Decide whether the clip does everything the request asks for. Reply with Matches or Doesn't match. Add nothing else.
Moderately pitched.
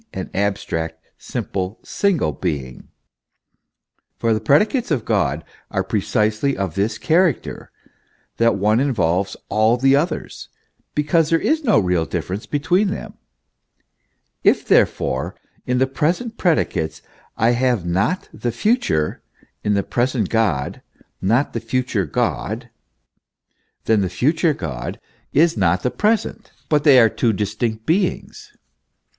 Doesn't match